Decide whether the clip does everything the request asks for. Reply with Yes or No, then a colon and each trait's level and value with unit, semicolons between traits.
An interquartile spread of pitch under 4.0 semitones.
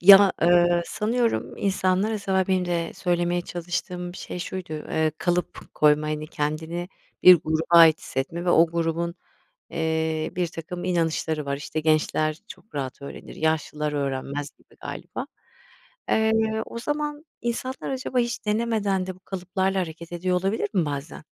Yes: average, 3.3 semitones